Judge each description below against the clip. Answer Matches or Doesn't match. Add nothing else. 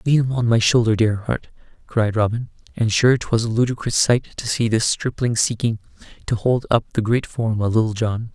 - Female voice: Doesn't match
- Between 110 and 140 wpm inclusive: Doesn't match